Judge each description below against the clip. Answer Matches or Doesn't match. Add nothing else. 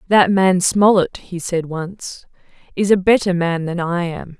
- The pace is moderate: Matches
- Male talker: Doesn't match